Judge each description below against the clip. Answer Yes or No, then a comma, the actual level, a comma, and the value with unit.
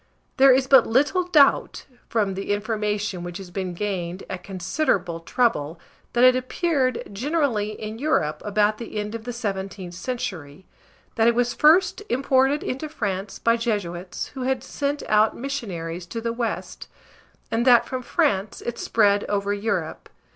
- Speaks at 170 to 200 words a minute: No, average, 160 wpm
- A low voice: No, high, 220 Hz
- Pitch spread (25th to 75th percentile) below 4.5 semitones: No, average, 4.8 semitones